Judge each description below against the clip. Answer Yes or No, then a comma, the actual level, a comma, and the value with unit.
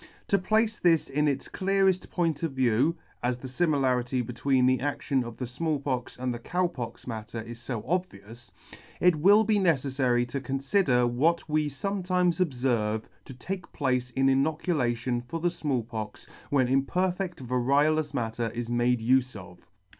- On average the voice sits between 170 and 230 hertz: No, low, 135 Hz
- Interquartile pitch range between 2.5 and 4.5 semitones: No, wide, 5.4 semitones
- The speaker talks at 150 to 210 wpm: Yes, average, 170 wpm